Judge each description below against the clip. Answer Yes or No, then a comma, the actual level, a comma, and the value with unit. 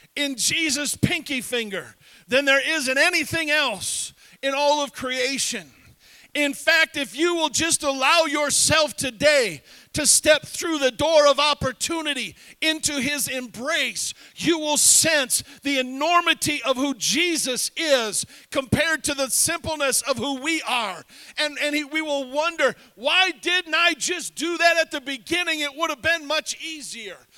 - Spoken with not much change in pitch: No, average, 3.0 semitones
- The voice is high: Yes, very high, 295 Hz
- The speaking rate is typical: Yes, average, 155 wpm